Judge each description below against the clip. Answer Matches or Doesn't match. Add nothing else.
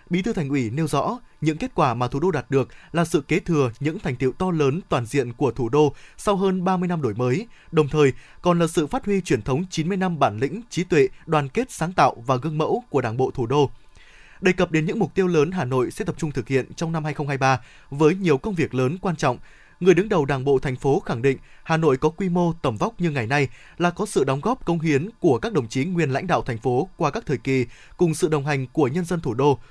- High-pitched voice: Doesn't match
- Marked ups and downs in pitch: Doesn't match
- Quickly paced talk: Matches